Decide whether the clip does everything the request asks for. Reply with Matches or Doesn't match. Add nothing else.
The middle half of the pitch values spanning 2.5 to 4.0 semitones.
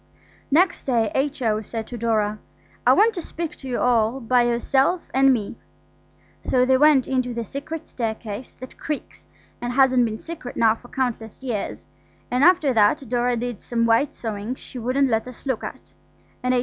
Matches